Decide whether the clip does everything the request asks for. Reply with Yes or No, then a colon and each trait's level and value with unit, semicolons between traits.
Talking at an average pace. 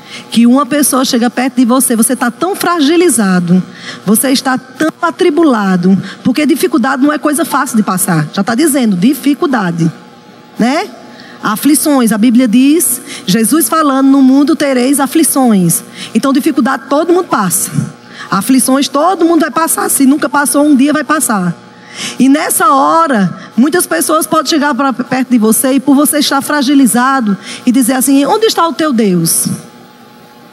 Yes: average, 155 wpm